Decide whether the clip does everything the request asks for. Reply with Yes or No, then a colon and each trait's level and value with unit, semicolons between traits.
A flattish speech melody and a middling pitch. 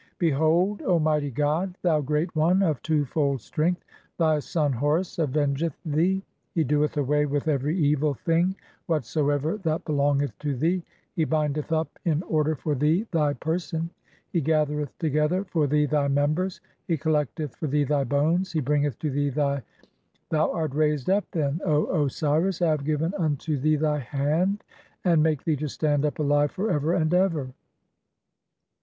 Yes: narrow, 2.2 semitones; medium, 155 Hz